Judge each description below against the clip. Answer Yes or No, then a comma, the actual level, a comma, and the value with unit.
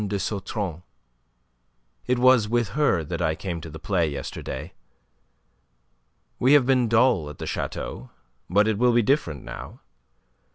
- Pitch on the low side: Yes, low, 100 Hz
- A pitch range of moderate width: No, wide, 7.0 semitones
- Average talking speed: Yes, average, 150 wpm